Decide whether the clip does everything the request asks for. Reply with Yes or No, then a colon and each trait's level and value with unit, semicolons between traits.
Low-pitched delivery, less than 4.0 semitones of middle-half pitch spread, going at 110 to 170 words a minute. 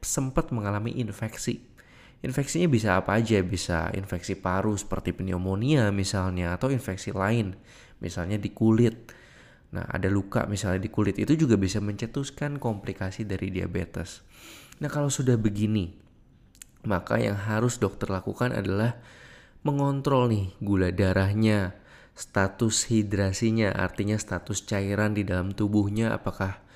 Yes: low, 105 Hz; average, 3.4 semitones; average, 125 wpm